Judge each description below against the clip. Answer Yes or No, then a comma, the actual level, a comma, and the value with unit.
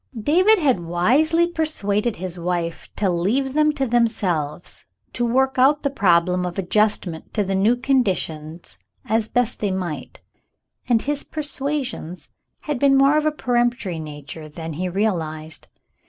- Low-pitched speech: No, high, 215 Hz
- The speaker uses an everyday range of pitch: No, wide, 7.6 semitones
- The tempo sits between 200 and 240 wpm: No, average, 145 wpm